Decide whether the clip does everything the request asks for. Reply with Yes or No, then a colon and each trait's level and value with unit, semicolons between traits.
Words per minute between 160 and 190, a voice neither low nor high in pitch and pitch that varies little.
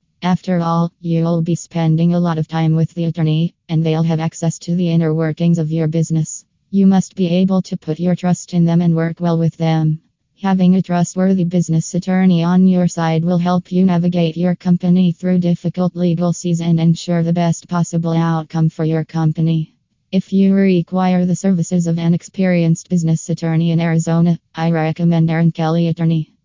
Yes: average, 185 wpm; medium, 170 Hz; narrow, 1.5 semitones